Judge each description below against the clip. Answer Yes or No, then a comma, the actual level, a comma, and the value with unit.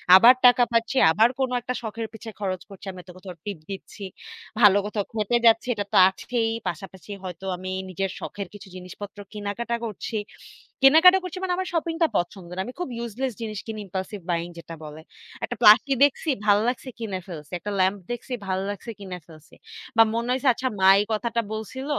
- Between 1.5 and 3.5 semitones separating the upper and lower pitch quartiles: No, average, 3.9 semitones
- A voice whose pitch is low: No, high, 210 Hz